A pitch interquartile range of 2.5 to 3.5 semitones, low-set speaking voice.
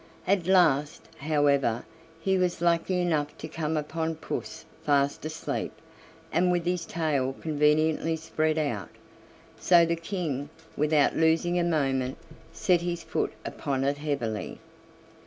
No: average, 2.9 semitones; medium, 155 Hz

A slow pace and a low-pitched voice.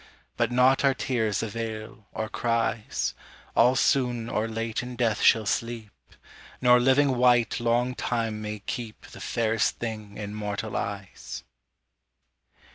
Yes: slow, 130 wpm; low, 115 Hz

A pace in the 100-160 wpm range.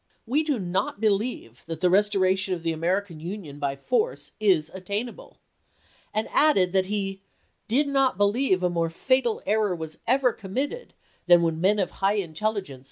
No: average, 170 wpm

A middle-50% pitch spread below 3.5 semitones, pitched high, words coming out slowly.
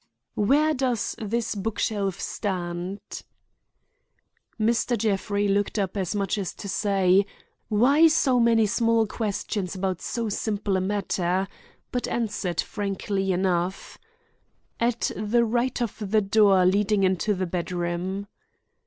Yes: average, 3.0 semitones; high, 205 Hz; slow, 125 wpm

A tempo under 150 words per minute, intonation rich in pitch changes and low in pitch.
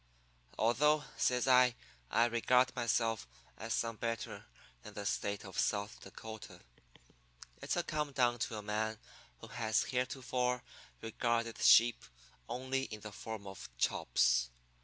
No: slow, 135 wpm; average, 2.7 semitones; low, 115 Hz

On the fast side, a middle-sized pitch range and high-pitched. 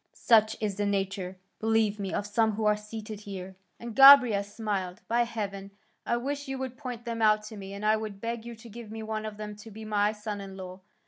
No: fast, 235 wpm; narrow, 2.2 semitones; high, 215 Hz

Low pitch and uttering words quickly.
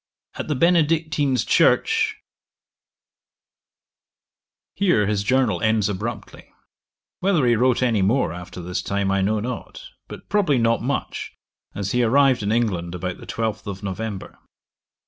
No: low, 110 Hz; average, 140 wpm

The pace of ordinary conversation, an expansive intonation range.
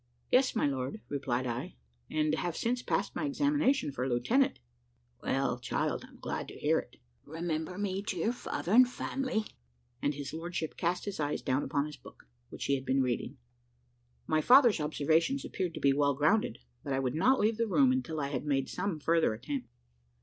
Yes: average, 195 wpm; wide, 8.0 semitones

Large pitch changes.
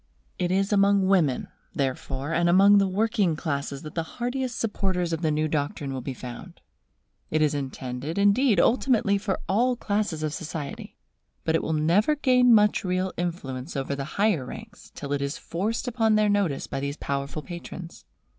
Yes: wide, 6.1 semitones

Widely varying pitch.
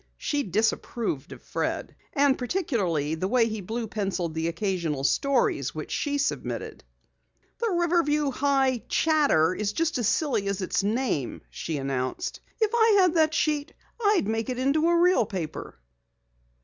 Yes: wide, 8.5 semitones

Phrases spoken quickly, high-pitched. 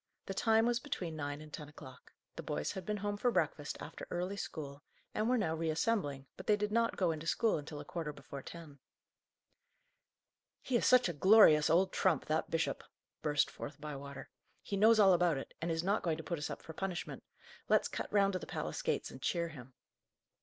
No: fast, 210 wpm; medium, 170 Hz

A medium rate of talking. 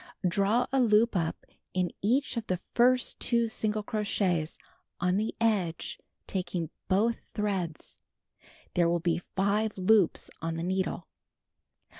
No: slow, 130 wpm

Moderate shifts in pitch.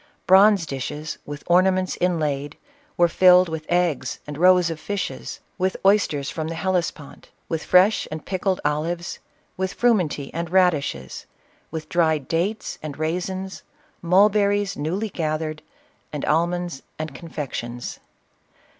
Yes: average, 3.4 semitones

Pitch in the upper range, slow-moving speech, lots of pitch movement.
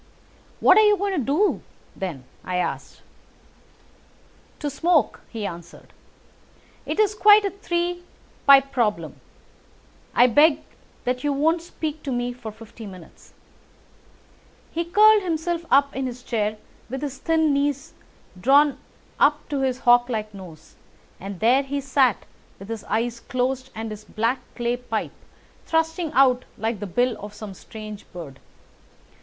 No: very high, 255 Hz; average, 150 wpm; wide, 6.0 semitones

